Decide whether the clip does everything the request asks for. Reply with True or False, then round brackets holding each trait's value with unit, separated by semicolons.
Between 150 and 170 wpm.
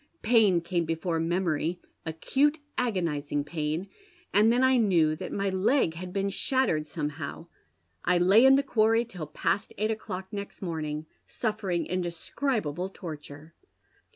False (135 wpm)